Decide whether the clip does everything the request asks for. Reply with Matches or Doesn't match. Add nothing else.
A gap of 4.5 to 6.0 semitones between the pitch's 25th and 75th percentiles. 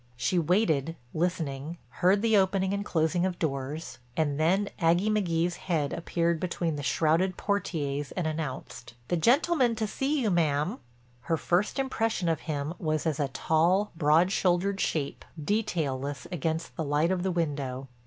Doesn't match